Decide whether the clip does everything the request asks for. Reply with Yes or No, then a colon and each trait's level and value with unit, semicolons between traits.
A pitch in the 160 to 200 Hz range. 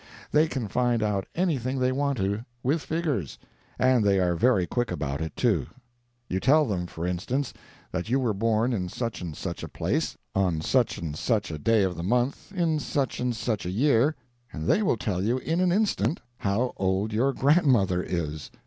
No: low, 115 Hz